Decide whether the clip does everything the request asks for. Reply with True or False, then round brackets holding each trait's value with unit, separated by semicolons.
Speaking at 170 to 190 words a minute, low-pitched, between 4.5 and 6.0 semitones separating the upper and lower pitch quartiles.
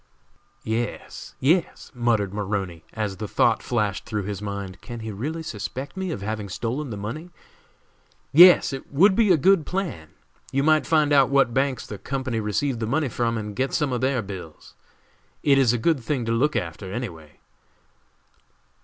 True (180 wpm; 120 Hz; 5.5 semitones)